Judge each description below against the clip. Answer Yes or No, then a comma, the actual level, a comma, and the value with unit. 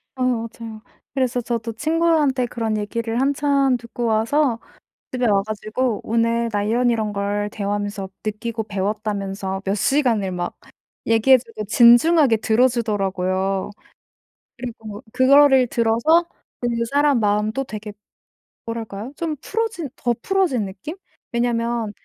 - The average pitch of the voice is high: Yes, high, 230 Hz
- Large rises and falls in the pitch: No, average, 3.5 semitones